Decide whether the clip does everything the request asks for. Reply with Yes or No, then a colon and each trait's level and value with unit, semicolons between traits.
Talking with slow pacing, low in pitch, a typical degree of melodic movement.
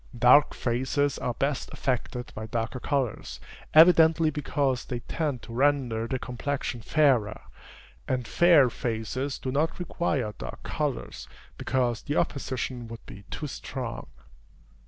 Yes: slow, 130 wpm; low, 130 Hz; average, 3.4 semitones